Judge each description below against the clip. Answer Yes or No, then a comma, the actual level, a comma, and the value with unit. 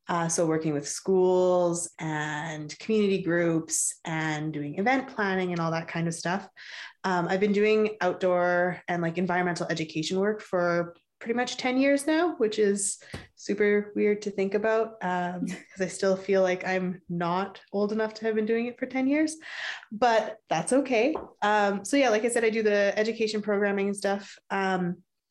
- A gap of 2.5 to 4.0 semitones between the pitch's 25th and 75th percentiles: Yes, average, 3.7 semitones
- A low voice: No, high, 195 Hz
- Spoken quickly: No, average, 180 wpm